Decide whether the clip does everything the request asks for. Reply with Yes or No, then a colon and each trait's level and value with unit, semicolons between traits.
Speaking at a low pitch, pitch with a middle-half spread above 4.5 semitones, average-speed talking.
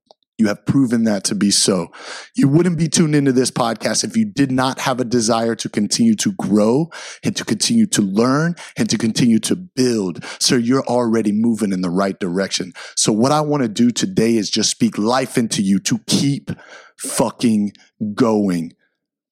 Yes: low, 120 Hz; average, 5.3 semitones; average, 185 wpm